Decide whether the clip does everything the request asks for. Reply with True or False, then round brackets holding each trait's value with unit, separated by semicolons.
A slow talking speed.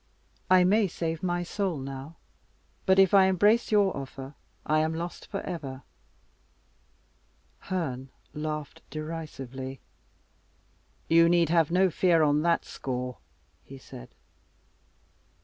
True (115 wpm)